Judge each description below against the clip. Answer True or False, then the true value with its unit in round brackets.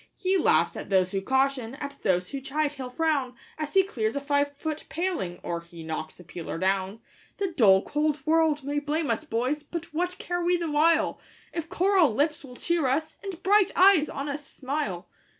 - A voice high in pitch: True (290 Hz)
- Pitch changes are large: True (6.0 semitones)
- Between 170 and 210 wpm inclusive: True (200 wpm)